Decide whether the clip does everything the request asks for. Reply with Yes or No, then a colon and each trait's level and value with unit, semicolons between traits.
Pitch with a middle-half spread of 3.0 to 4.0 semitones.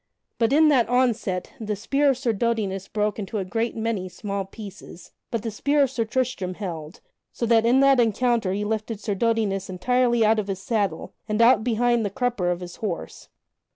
Yes: average, 3.5 semitones